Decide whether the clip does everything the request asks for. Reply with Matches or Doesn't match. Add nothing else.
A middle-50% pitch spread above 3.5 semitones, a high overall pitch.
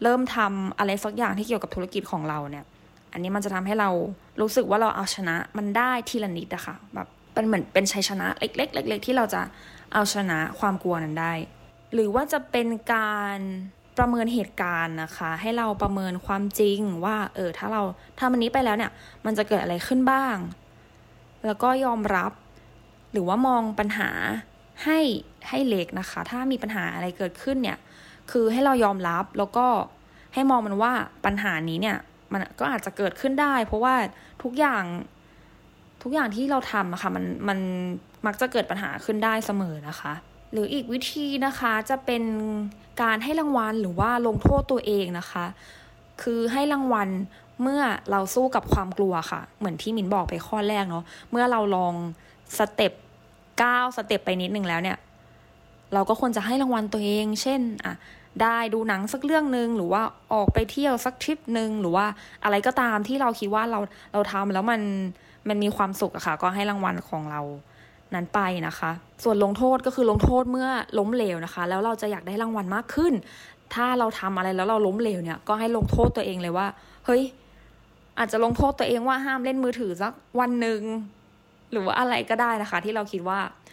Matches